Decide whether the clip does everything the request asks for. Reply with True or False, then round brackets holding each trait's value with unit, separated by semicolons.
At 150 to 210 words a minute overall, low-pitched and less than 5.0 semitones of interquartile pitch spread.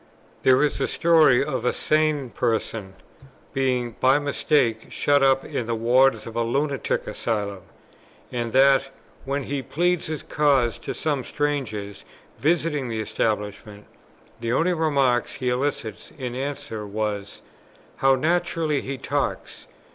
False (135 wpm; 130 Hz; 4.1 semitones)